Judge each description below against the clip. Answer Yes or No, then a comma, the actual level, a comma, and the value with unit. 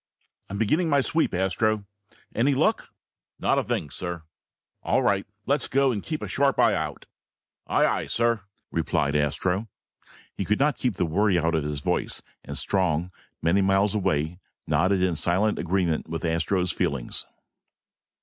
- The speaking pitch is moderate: No, very low, 95 Hz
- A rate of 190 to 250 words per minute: No, average, 160 wpm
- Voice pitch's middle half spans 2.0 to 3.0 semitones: No, average, 4.7 semitones